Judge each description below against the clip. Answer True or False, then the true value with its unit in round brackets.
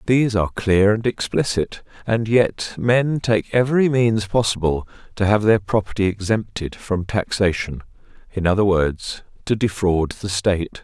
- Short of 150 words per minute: True (140 wpm)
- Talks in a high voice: False (105 Hz)